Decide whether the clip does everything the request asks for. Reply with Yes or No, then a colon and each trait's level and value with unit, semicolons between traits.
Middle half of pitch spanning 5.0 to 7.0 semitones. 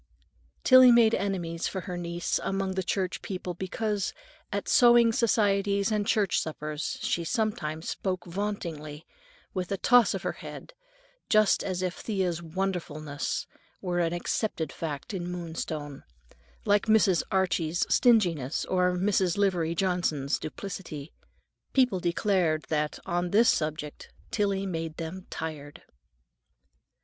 No: average, 3.6 semitones